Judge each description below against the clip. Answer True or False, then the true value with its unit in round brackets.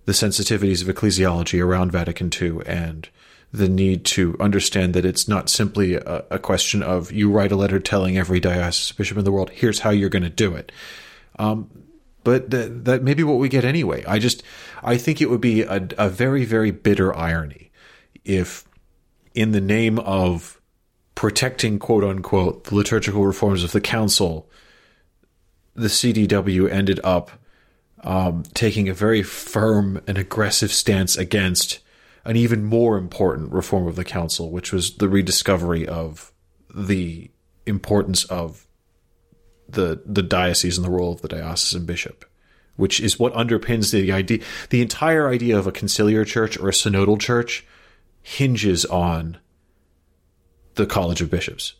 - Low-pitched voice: True (100 Hz)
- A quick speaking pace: False (160 wpm)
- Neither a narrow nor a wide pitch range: True (3.2 semitones)